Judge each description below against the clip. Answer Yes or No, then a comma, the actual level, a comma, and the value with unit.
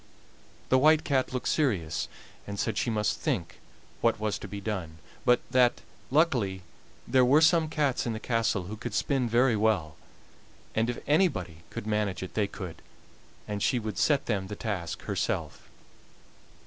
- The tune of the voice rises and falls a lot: No, average, 4.4 semitones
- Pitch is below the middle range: Yes, low, 110 Hz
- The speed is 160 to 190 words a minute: Yes, average, 165 wpm